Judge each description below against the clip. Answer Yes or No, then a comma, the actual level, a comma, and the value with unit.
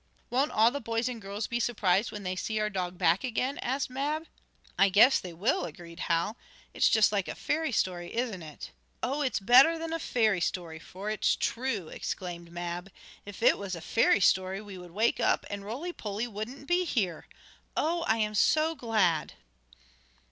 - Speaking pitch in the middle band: No, high, 215 Hz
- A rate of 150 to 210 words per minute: Yes, average, 190 wpm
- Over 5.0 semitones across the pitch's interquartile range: Yes, wide, 5.5 semitones